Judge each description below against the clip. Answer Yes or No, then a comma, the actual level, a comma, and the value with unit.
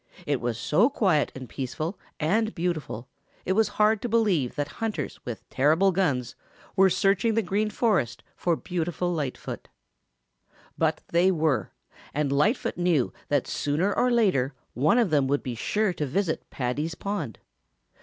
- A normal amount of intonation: No, wide, 6.3 semitones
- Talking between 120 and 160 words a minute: Yes, average, 155 wpm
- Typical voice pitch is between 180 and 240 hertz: No, medium, 165 Hz